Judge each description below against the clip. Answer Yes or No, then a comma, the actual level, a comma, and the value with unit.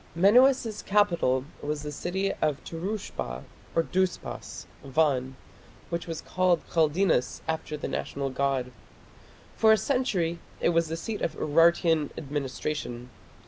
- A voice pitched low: No, medium, 165 Hz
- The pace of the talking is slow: Yes, slow, 125 wpm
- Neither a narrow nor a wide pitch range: Yes, average, 4.7 semitones